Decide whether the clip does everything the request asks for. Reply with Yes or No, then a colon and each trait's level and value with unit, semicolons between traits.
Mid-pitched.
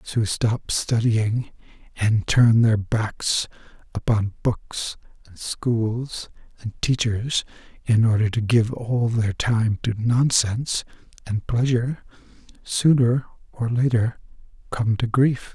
No: low, 115 Hz